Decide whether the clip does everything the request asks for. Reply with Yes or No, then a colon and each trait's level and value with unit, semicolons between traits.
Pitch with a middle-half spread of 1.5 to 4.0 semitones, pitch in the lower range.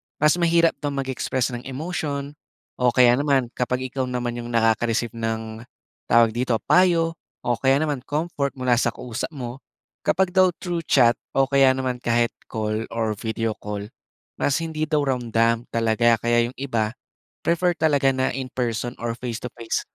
Yes: average, 3.6 semitones; low, 125 Hz